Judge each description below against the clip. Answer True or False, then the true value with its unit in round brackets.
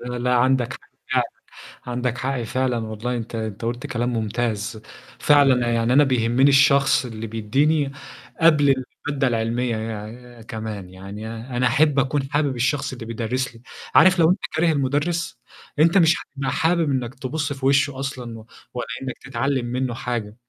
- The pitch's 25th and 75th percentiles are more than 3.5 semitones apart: False (3.2 semitones)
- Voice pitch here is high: False (125 Hz)